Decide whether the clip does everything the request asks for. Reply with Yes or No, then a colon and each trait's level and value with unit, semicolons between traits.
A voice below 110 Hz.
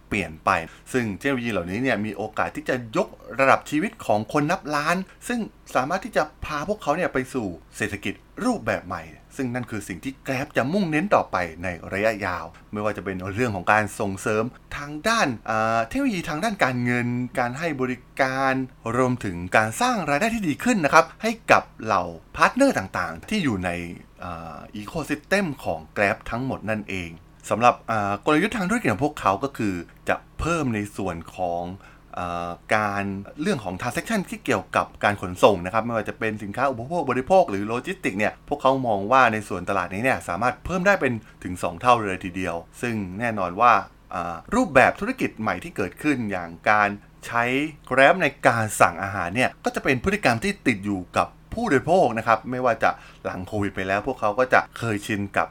No: low, 120 Hz